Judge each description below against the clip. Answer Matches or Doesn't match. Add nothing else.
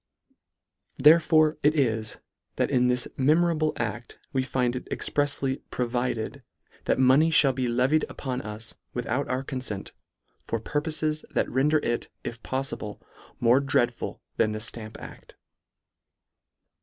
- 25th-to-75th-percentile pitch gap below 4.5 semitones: Matches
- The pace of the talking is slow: Matches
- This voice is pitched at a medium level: Doesn't match